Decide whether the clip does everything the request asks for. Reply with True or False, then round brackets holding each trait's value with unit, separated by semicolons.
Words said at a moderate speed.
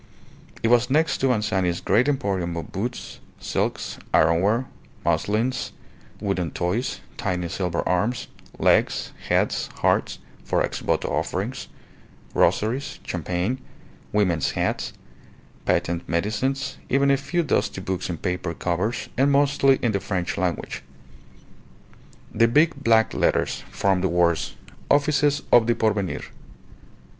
False (120 wpm)